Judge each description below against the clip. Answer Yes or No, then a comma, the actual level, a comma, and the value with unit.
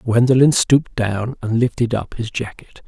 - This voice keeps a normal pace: Yes, average, 165 wpm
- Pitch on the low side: Yes, low, 120 Hz